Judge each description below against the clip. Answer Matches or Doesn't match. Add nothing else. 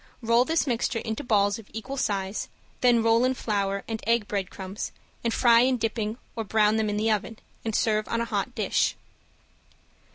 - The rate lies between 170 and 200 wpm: Matches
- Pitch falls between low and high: Doesn't match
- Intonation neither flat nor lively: Doesn't match